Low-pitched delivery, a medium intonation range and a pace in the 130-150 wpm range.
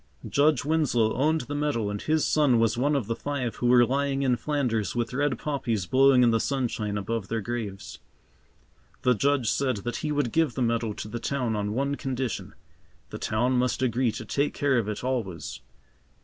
No: low, 125 Hz; average, 3.7 semitones; average, 195 wpm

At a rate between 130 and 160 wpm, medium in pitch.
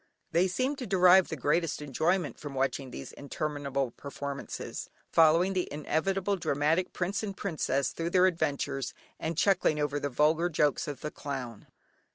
Yes: average, 155 wpm; medium, 155 Hz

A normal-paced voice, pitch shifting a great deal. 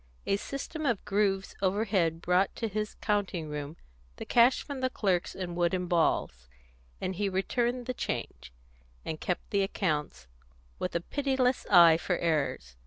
No: average, 155 wpm; average, 4.3 semitones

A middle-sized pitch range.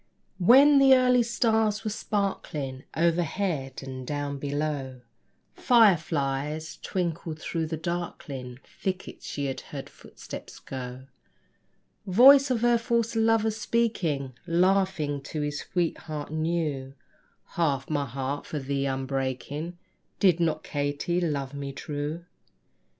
No: wide, 5.9 semitones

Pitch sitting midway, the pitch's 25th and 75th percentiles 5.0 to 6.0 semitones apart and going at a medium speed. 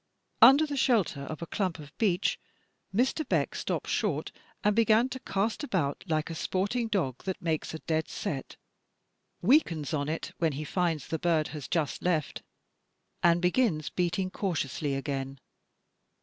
Yes: medium, 170 Hz; average, 5.3 semitones; average, 155 wpm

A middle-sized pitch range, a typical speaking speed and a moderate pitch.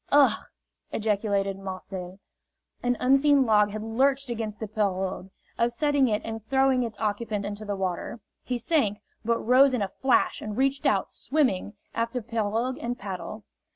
No: average, 3.9 semitones; average, 155 wpm; high, 225 Hz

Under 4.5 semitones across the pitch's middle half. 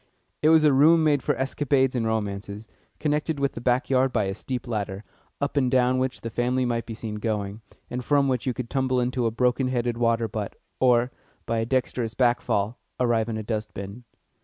Yes: average, 2.7 semitones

